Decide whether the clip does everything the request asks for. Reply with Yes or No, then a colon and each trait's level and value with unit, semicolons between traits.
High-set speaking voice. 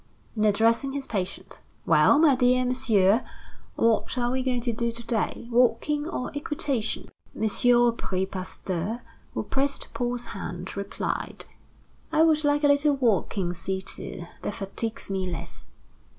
Yes: high, 235 Hz